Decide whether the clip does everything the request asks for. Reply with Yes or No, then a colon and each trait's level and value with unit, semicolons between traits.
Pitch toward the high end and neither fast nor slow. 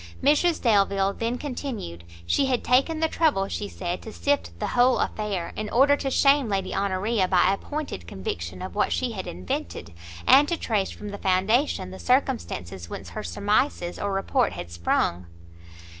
Yes: high, 200 Hz; average, 175 wpm